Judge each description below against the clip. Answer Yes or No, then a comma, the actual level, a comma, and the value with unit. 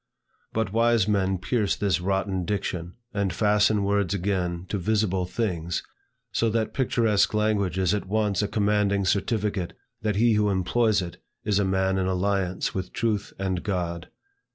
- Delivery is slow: No, average, 155 wpm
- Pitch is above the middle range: No, low, 100 Hz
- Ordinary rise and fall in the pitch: No, narrow, 2.3 semitones